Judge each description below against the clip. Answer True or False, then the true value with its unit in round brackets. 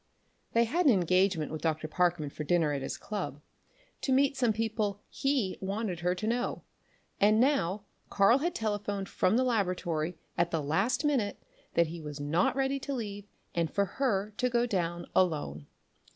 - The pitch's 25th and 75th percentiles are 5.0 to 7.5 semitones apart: True (5.6 semitones)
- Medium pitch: False (195 Hz)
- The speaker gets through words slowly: False (180 wpm)